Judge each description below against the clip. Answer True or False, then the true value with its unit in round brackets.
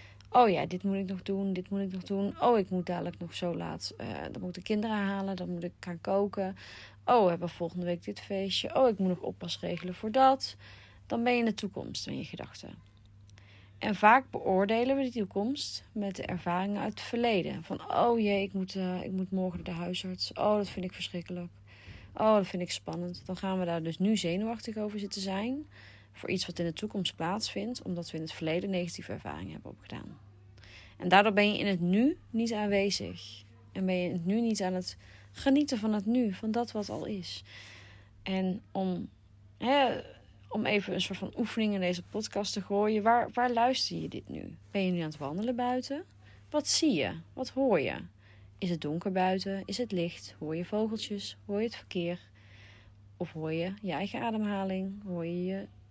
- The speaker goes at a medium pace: False (210 wpm)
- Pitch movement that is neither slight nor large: True (4.6 semitones)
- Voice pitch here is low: False (185 Hz)